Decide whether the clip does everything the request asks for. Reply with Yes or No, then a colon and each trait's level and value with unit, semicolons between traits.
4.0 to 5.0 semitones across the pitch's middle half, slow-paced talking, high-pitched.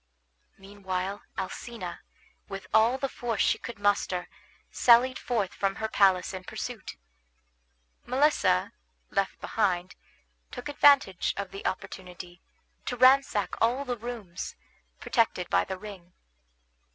Yes: average, 4.5 semitones; slow, 115 wpm; high, 205 Hz